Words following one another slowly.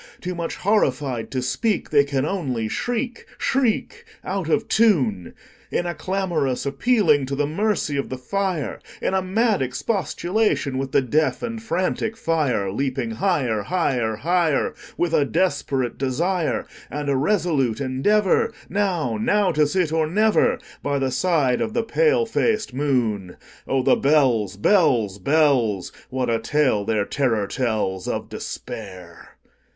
Yes: slow, 120 wpm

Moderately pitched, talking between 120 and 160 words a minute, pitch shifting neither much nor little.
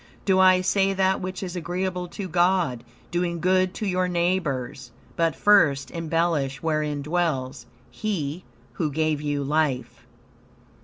Yes: medium, 170 Hz; slow, 135 wpm; average, 4.1 semitones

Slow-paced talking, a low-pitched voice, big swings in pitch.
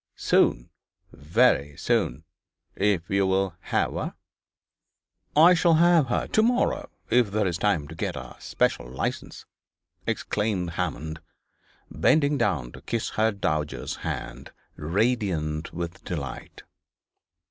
Yes: slow, 120 wpm; very low, 95 Hz; wide, 6.9 semitones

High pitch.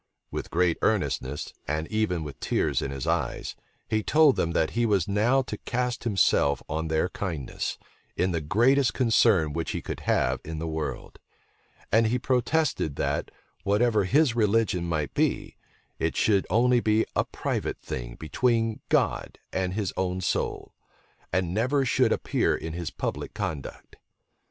No: low, 100 Hz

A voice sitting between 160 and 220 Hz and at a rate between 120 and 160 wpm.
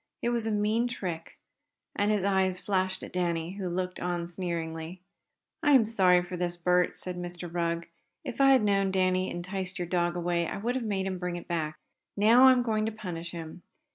No: medium, 185 Hz; fast, 205 wpm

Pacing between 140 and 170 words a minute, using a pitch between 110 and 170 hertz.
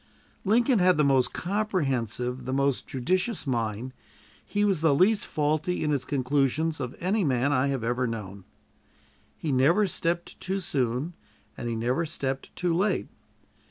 Yes: average, 155 wpm; medium, 140 Hz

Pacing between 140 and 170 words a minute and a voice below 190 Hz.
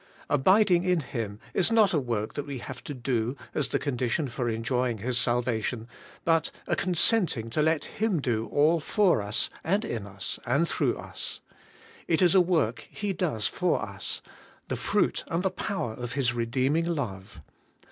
No: average, 180 wpm; low, 135 Hz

